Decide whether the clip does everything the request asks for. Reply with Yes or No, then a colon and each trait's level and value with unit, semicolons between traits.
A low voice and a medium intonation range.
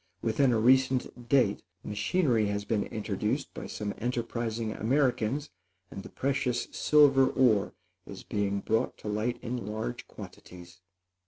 Yes: low, 115 Hz; average, 3.7 semitones